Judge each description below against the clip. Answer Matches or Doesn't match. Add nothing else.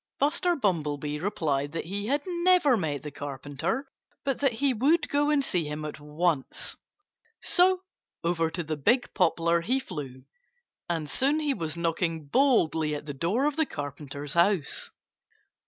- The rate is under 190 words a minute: Matches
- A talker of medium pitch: Matches